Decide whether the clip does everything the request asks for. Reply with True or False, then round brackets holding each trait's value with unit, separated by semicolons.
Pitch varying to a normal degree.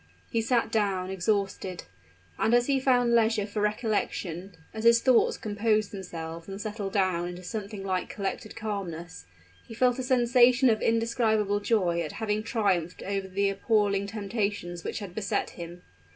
True (3.1 semitones)